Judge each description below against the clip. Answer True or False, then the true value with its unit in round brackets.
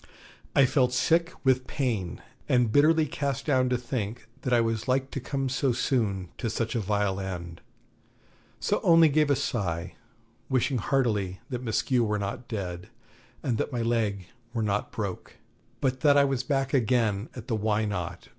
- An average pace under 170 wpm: False (175 wpm)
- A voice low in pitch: True (120 Hz)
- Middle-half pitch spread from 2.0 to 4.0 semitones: False (4.4 semitones)